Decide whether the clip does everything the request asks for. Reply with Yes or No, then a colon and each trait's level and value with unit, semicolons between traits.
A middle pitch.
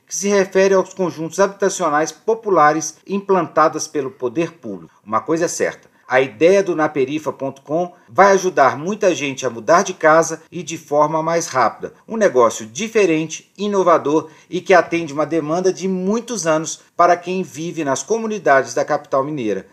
Yes: medium, 165 Hz